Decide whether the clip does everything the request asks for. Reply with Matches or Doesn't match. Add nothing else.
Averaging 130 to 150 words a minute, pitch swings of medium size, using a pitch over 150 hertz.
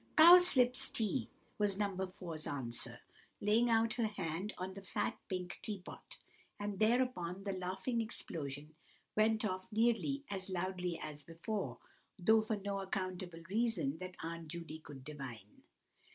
Matches